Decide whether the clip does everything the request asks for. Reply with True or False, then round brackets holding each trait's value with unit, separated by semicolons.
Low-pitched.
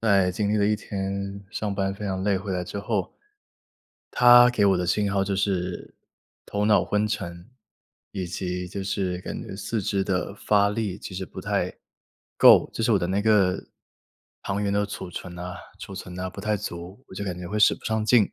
True (100 Hz)